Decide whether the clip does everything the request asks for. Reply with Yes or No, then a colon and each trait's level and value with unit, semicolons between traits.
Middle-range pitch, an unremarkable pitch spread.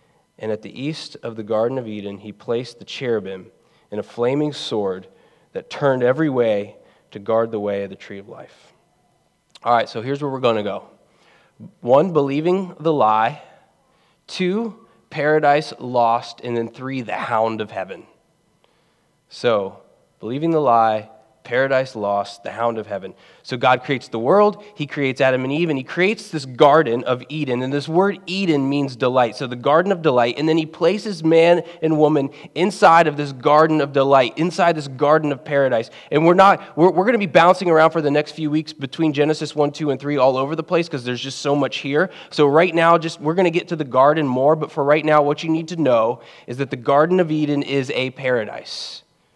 Yes: medium, 145 Hz; average, 4.5 semitones